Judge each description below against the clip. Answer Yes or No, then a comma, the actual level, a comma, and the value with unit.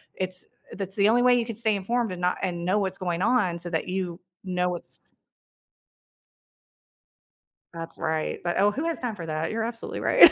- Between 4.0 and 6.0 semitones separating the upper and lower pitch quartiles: Yes, average, 4.3 semitones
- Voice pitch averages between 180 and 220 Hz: Yes, high, 190 Hz